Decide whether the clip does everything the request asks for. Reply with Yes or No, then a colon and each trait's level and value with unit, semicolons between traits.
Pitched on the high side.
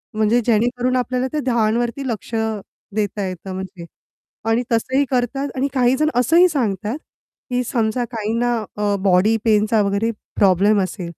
Yes: high, 225 Hz